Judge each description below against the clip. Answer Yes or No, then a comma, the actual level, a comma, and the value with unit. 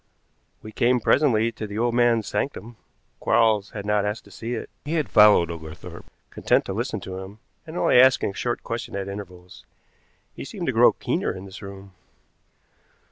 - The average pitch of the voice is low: Yes, low, 105 Hz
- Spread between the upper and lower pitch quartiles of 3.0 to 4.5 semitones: Yes, average, 3.3 semitones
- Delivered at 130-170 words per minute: No, average, 185 wpm